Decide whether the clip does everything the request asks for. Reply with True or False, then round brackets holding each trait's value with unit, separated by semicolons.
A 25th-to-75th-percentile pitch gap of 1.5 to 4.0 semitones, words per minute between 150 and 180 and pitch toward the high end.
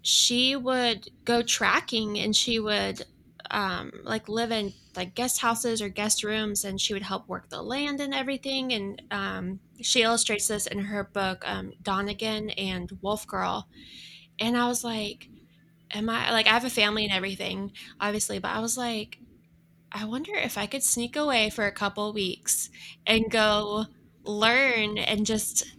True (2.6 semitones; 170 wpm; 215 Hz)